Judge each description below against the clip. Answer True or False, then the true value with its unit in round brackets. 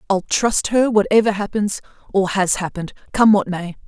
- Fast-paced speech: False (170 wpm)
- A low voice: False (200 Hz)